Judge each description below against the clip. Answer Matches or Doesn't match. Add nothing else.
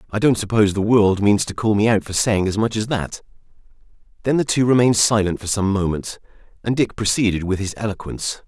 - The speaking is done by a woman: Doesn't match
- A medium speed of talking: Doesn't match